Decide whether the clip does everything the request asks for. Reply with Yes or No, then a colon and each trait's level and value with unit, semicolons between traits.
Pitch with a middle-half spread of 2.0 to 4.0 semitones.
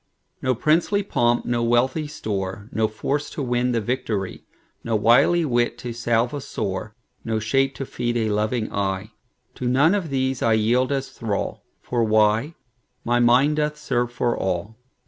Yes: average, 3.4 semitones